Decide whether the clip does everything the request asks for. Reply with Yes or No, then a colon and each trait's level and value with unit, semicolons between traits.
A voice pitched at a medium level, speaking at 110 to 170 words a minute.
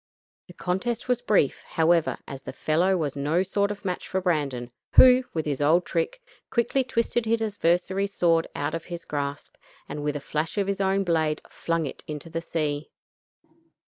No: medium, 170 Hz; average, 180 wpm